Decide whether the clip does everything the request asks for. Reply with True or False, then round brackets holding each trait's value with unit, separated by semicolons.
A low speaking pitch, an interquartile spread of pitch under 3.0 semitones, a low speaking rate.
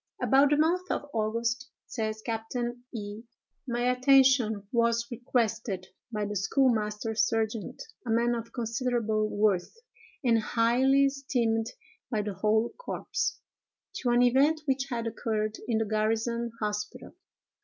False (230 Hz; 2.5 semitones; 130 wpm)